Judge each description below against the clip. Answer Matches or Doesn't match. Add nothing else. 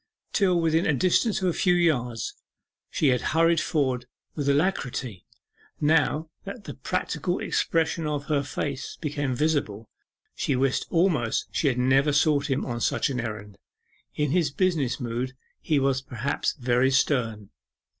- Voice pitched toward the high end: Doesn't match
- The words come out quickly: Doesn't match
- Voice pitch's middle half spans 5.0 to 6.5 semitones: Doesn't match